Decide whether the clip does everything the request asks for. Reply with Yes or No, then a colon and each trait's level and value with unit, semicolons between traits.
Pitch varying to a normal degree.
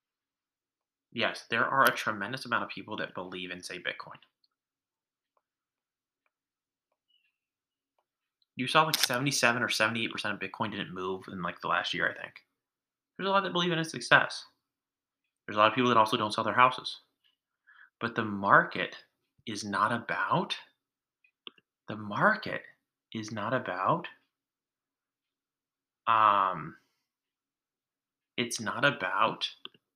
Yes: average, 3.3 semitones